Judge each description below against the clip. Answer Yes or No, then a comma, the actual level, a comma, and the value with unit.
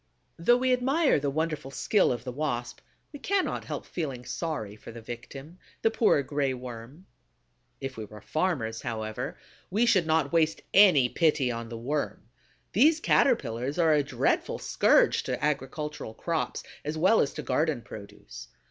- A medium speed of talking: Yes, average, 160 wpm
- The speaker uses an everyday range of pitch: No, wide, 5.9 semitones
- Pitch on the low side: No, medium, 150 Hz